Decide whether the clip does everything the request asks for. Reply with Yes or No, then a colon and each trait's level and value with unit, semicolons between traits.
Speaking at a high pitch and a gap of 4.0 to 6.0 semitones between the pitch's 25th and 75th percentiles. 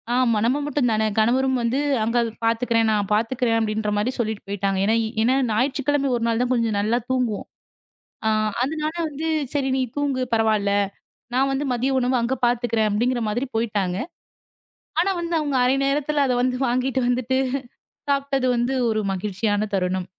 No: high, 240 Hz; average, 3.3 semitones